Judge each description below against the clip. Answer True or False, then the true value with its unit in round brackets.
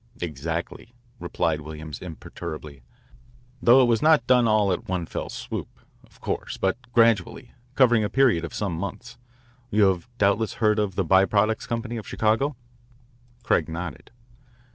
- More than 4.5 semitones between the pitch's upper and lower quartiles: True (5.3 semitones)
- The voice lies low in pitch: True (105 Hz)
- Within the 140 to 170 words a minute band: True (150 wpm)